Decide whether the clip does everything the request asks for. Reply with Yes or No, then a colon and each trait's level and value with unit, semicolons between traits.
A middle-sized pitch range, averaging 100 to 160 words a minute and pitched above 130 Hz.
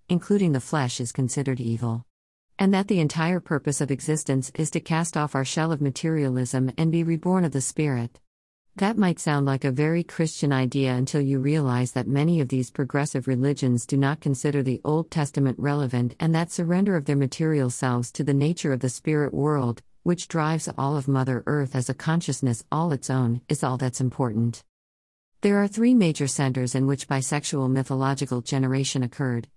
No: average, 3.6 semitones; average, 185 wpm; medium, 140 Hz